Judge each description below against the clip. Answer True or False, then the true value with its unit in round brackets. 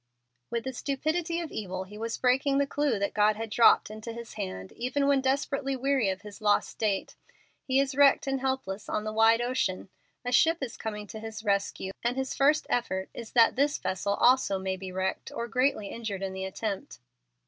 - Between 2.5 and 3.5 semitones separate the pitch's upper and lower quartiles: False (4.8 semitones)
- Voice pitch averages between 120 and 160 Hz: False (230 Hz)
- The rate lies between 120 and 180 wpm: False (205 wpm)